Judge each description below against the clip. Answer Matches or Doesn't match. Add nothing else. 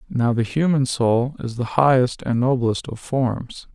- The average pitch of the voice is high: Doesn't match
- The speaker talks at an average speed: Matches